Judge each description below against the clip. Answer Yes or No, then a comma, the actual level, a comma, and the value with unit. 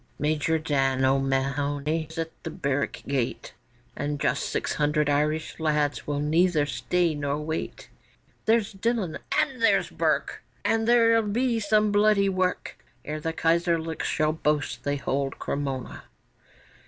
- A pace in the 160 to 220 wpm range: No, slow, 135 wpm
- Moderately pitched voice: Yes, medium, 155 Hz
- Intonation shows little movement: No, average, 5.0 semitones